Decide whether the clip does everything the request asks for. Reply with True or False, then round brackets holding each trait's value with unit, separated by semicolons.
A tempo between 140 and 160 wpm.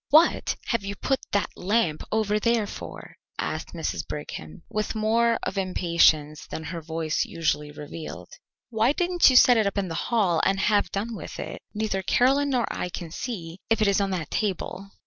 False (185 wpm)